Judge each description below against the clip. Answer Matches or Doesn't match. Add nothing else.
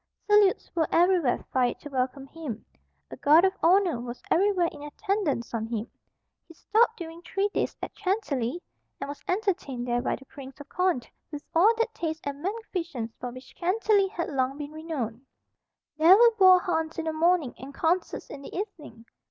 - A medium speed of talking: Matches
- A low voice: Doesn't match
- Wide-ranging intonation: Matches